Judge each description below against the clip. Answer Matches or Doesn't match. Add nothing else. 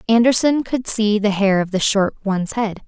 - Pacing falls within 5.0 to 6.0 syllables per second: Matches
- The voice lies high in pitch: Matches